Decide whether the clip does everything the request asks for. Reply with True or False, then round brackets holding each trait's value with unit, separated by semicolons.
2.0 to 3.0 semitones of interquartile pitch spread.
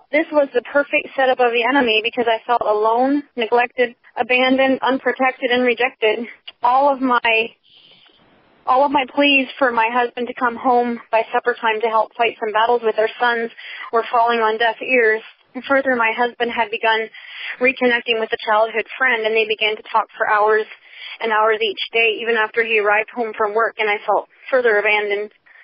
True (2.4 semitones)